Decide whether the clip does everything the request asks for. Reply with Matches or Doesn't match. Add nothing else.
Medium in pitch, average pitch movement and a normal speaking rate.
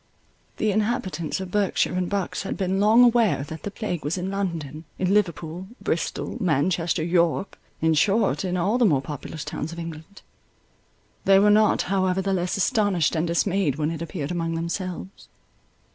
Matches